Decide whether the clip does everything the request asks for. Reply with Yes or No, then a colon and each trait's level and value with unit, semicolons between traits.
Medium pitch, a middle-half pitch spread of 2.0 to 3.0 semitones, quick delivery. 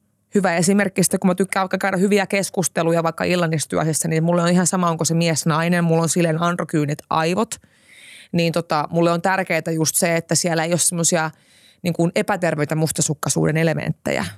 Yes: medium, 170 Hz; narrow, 2.4 semitones; fast, 175 wpm